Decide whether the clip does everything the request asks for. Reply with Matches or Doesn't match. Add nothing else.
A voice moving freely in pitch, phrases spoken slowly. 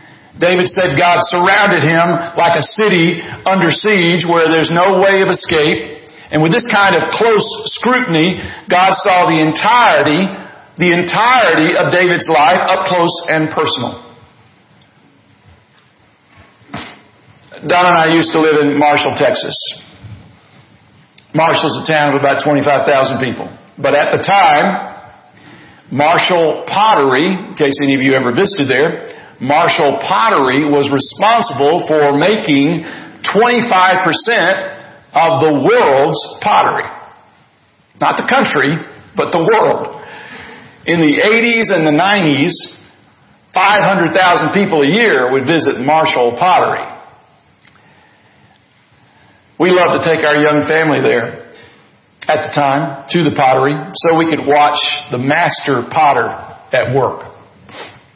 Doesn't match